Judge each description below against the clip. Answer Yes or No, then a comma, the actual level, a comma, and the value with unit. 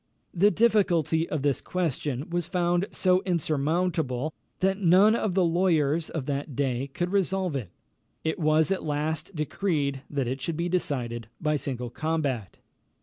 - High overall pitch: No, medium, 160 Hz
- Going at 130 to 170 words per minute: Yes, average, 150 wpm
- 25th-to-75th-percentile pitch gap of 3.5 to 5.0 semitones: Yes, average, 4.4 semitones